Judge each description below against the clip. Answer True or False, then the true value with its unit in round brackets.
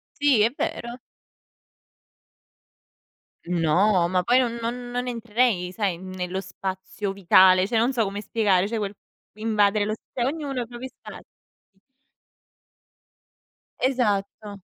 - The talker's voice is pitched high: True (215 Hz)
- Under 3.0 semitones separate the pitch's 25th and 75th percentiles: False (4.1 semitones)